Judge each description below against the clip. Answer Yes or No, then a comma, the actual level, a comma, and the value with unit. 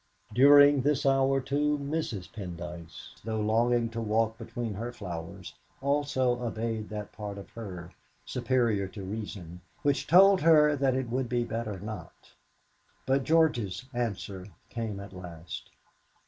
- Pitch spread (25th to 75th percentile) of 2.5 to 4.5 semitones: No, average, 5.1 semitones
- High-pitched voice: No, low, 115 Hz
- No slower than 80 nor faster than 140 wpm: Yes, slow, 135 wpm